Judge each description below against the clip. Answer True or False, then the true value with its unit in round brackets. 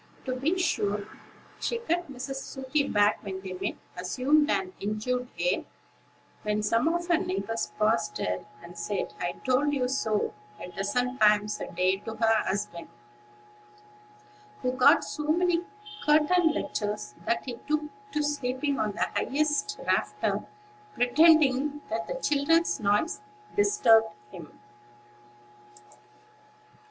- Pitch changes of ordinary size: False (6.5 semitones)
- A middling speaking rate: False (130 wpm)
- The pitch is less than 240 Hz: False (255 Hz)